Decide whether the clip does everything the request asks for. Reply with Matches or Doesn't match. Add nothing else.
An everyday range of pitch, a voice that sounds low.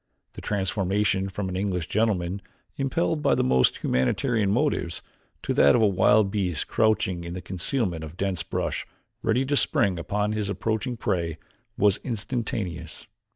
Matches